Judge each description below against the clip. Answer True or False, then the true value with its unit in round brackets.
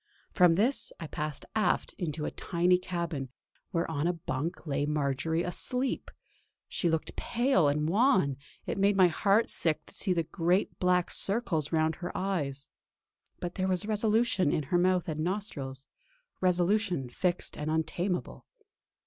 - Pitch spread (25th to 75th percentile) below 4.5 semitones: True (3.7 semitones)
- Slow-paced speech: False (150 wpm)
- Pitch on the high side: False (175 Hz)